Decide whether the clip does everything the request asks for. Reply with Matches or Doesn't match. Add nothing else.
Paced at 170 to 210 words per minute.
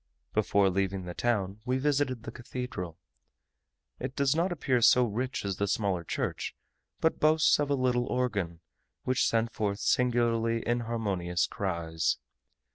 Doesn't match